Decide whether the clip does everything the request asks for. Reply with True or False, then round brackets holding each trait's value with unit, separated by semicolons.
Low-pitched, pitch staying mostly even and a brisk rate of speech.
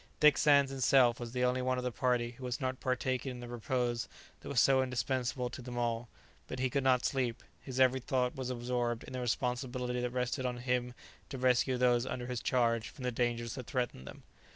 True (125 Hz; 1.1 semitones; 220 wpm)